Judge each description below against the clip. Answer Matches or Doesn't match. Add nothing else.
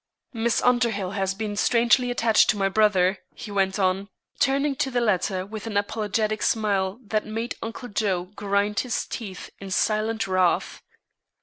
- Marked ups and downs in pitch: Doesn't match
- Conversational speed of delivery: Matches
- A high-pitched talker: Matches